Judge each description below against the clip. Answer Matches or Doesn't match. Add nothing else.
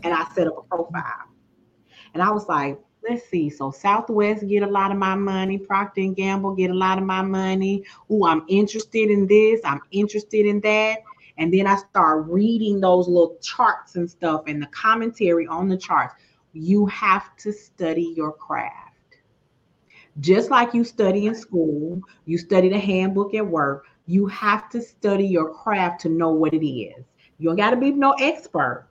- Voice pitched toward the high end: Matches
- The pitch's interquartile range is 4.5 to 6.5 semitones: Doesn't match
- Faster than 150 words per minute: Matches